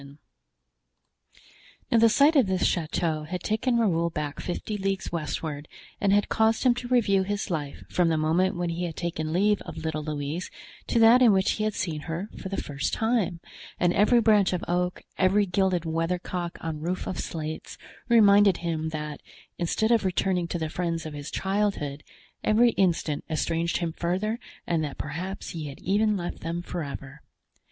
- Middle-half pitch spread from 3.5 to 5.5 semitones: Yes, average, 4.2 semitones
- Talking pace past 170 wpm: Yes, average, 180 wpm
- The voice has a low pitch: No, medium, 175 Hz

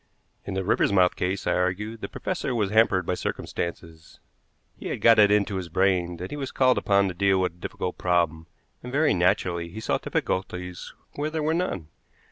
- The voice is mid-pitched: No, very low, 95 Hz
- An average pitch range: Yes, average, 3.5 semitones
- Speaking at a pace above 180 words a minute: Yes, average, 195 wpm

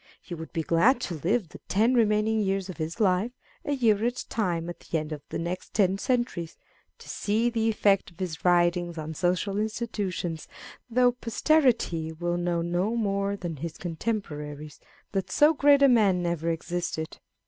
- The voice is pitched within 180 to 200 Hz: Yes, medium, 185 Hz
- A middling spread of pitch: Yes, average, 4.8 semitones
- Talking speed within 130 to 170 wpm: No, average, 180 wpm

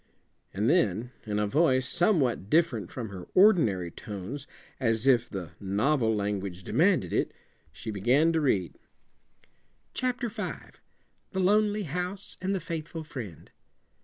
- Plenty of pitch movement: Yes, wide, 8.8 semitones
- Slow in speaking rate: Yes, slow, 130 wpm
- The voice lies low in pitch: Yes, low, 130 Hz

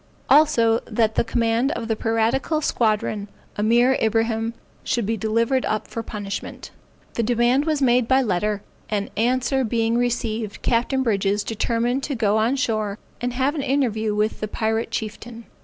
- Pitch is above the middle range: Yes, high, 230 Hz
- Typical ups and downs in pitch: No, narrow, 2.3 semitones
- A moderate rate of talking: Yes, average, 155 wpm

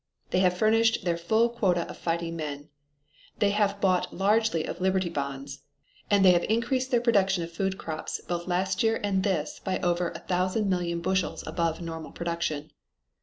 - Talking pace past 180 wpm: No, average, 175 wpm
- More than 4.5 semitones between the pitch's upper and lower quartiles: No, average, 3.1 semitones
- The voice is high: No, medium, 180 Hz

